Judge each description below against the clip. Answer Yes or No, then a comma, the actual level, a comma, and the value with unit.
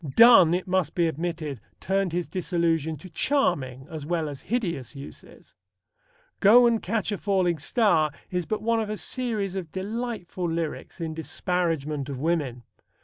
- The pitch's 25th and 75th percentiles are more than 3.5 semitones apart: Yes, average, 4.3 semitones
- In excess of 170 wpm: No, average, 155 wpm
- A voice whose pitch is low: No, medium, 175 Hz